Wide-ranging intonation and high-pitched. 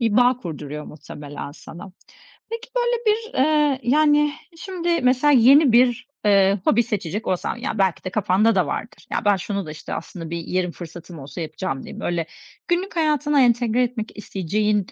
Yes: wide, 7.9 semitones; high, 220 Hz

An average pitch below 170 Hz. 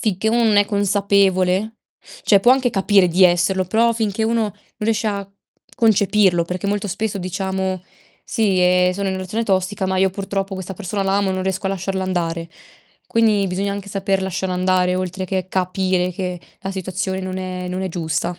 No: high, 190 Hz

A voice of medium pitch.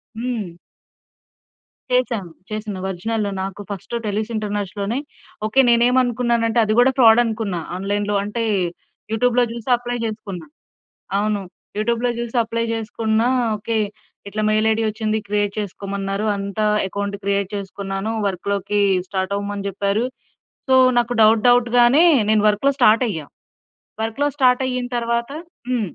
No: high, 215 Hz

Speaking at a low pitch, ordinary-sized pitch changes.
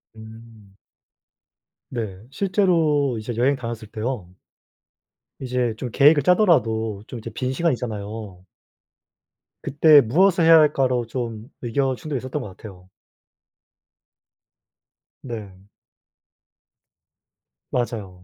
Yes: low, 120 Hz; average, 4.5 semitones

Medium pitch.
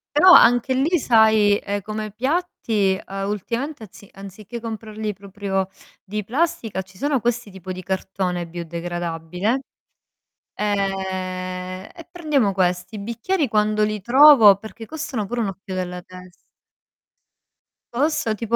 No: high, 210 Hz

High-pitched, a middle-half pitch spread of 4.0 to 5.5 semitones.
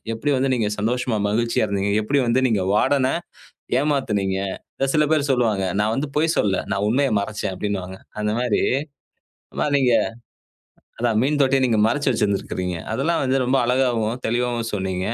No: low, 115 Hz; average, 4.4 semitones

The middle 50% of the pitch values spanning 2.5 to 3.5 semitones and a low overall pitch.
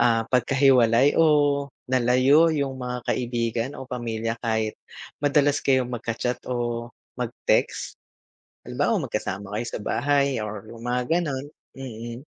Yes: average, 2.9 semitones; low, 125 Hz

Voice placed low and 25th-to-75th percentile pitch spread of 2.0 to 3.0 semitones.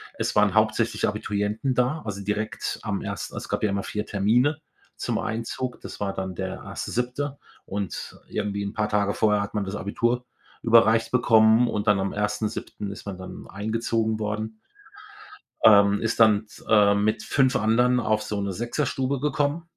Yes: low, 110 Hz; narrow, 2.5 semitones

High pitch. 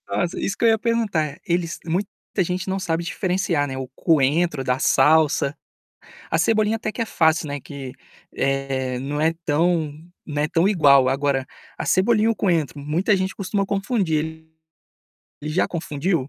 No: medium, 165 Hz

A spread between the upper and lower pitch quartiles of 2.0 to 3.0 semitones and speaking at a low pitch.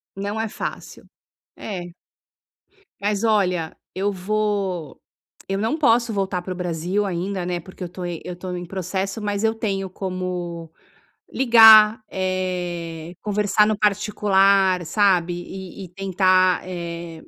No: narrow, 2.5 semitones; high, 190 Hz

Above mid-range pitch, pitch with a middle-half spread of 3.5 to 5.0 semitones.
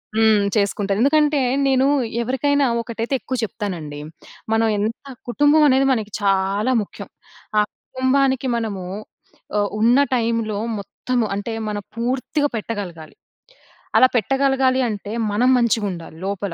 Yes: high, 230 Hz; average, 4.2 semitones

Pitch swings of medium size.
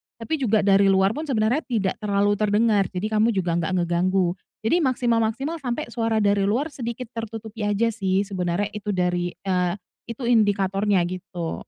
Yes: average, 3.2 semitones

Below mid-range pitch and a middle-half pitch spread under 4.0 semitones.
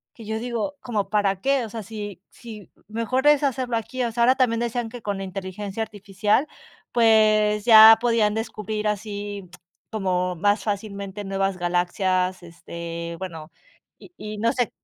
No: high, 210 Hz; average, 2.9 semitones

